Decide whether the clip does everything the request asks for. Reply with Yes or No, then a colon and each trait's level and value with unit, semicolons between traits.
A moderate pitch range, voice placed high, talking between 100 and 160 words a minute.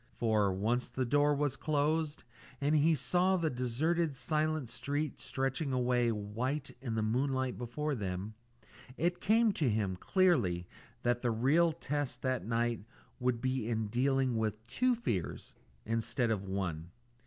No: average, 4.8 semitones; low, 125 Hz; average, 145 wpm